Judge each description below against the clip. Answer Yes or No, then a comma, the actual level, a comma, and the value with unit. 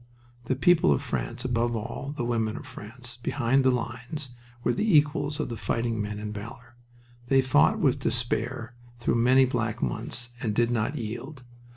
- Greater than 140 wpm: Yes, average, 175 wpm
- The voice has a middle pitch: No, low, 120 Hz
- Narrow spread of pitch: Yes, narrow, 2.1 semitones